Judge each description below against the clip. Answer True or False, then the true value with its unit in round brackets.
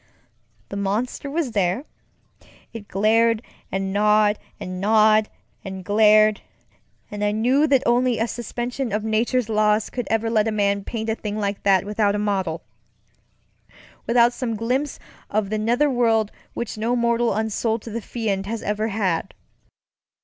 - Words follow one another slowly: False (145 wpm)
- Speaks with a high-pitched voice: True (215 Hz)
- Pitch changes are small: True (2.2 semitones)